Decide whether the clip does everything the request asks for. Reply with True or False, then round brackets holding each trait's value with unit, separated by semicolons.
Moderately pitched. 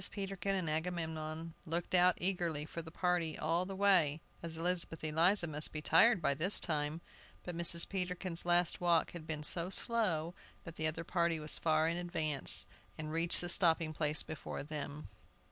True (165 Hz)